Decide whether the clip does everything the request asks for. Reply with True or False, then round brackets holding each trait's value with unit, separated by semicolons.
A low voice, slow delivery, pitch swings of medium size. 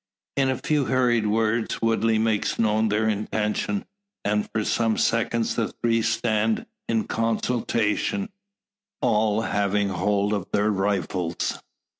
False (110 Hz; 125 wpm; 1.7 semitones)